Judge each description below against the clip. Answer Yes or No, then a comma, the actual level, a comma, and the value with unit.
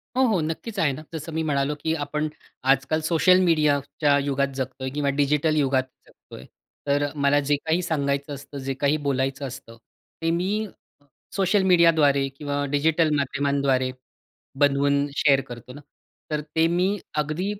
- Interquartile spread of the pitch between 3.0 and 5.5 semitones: No, narrow, 2.6 semitones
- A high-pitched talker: No, medium, 145 Hz